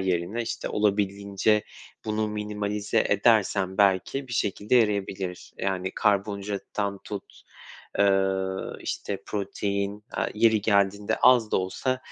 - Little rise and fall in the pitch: Yes, narrow, 1.4 semitones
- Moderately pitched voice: No, low, 100 Hz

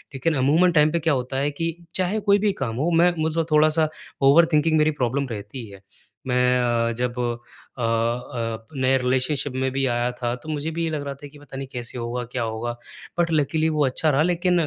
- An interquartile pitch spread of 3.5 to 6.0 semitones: Yes, average, 4.3 semitones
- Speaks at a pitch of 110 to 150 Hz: Yes, medium, 140 Hz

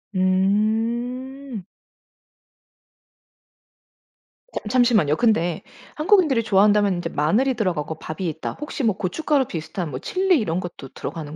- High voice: Yes, high, 210 Hz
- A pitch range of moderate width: No, wide, 6.6 semitones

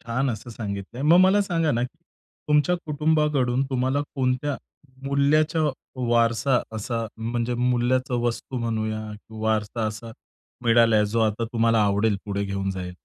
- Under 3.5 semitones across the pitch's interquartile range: No, average, 3.8 semitones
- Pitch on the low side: Yes, low, 120 Hz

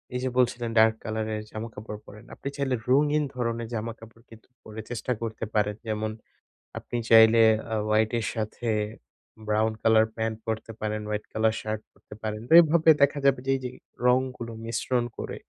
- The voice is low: Yes, low, 115 Hz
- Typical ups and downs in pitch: No, narrow, 2.1 semitones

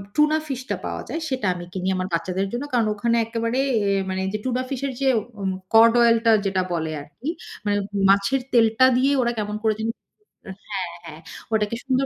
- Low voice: No, high, 225 Hz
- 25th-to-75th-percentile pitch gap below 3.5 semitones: No, average, 4.5 semitones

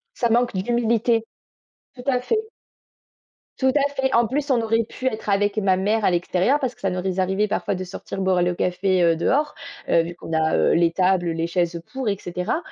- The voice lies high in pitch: Yes, high, 195 Hz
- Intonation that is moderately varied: Yes, average, 5.0 semitones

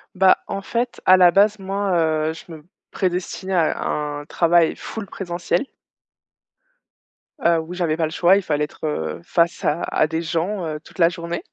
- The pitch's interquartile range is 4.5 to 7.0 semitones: No, average, 2.9 semitones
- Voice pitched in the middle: Yes, medium, 170 Hz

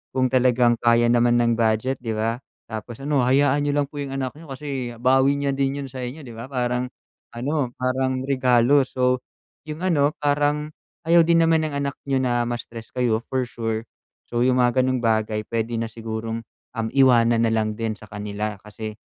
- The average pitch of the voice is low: Yes, low, 125 Hz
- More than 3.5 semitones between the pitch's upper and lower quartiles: No, average, 3.1 semitones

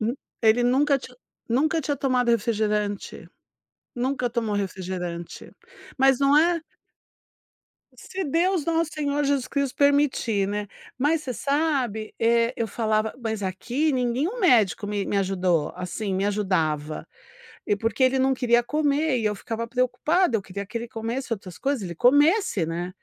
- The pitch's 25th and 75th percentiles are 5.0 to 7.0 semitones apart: Yes, wide, 5.6 semitones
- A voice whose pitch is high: Yes, high, 240 Hz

